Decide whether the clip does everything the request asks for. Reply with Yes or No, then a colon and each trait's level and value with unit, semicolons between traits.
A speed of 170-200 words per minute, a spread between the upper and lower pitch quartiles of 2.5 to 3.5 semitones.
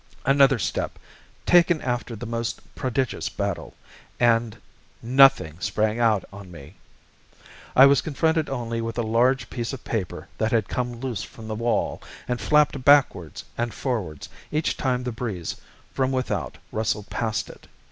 No: average, 150 wpm; average, 3.2 semitones